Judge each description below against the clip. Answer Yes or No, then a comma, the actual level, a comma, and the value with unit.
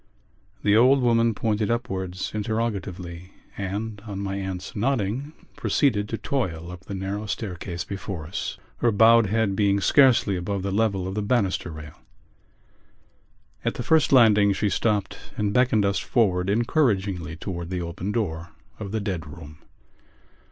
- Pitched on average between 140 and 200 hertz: No, low, 100 Hz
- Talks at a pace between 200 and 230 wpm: No, average, 150 wpm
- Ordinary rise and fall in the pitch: Yes, average, 3.4 semitones